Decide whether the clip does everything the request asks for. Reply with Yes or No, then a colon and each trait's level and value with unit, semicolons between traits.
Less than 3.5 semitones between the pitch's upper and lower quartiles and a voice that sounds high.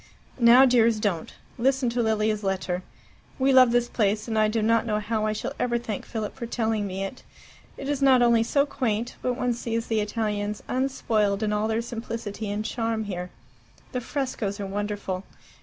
Yes: narrow, 2.5 semitones; high, 225 Hz